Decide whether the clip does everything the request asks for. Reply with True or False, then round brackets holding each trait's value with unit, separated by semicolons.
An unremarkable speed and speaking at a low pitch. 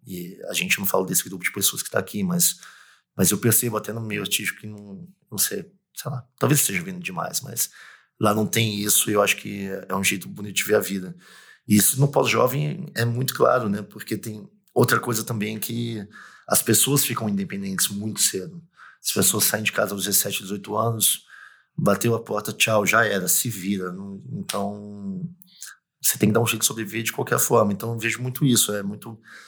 False (210 wpm; 115 Hz)